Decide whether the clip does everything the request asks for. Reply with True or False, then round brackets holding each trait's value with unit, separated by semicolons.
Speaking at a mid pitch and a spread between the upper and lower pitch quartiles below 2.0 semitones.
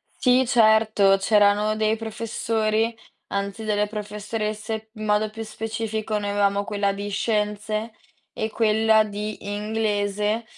False (215 Hz; 1.2 semitones)